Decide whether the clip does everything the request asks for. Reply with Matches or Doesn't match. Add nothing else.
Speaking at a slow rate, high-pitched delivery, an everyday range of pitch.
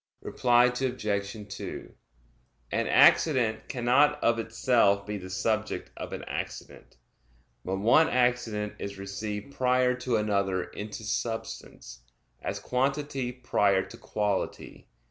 Doesn't match